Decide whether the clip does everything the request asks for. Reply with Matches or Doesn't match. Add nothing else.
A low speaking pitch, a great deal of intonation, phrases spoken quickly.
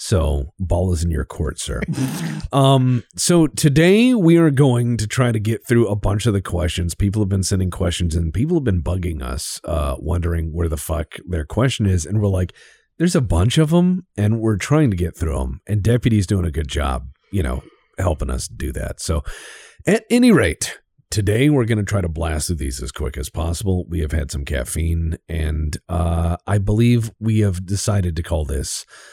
Matches